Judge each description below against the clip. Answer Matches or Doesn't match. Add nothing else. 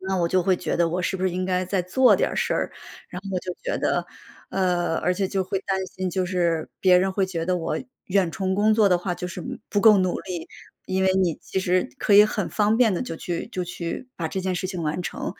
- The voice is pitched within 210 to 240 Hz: Doesn't match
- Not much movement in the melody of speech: Matches